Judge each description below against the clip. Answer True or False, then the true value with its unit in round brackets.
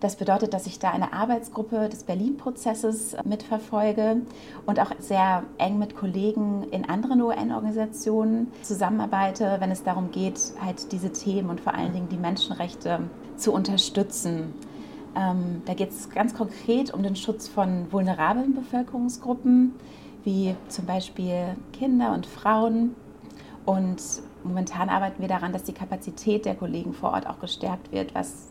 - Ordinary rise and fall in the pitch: True (3.2 semitones)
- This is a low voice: False (200 Hz)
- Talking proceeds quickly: False (145 wpm)